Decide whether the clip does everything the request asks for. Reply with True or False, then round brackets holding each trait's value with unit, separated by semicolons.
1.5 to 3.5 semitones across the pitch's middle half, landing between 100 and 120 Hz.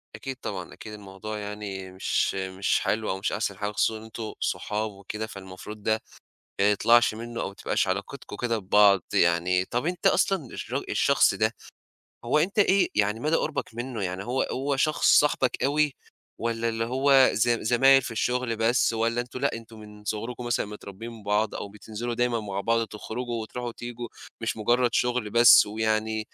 True (2.8 semitones; 110 Hz)